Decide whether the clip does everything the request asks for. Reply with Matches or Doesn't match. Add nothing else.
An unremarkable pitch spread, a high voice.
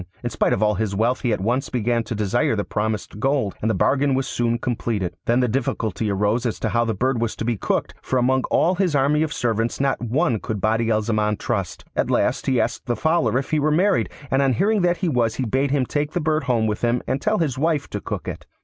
Doesn't match